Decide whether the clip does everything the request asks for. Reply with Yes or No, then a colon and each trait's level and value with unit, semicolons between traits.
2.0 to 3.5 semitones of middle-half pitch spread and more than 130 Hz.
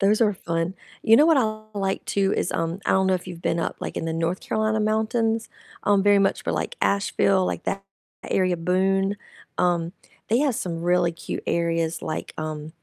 No: average, 4.1 semitones; high, 190 Hz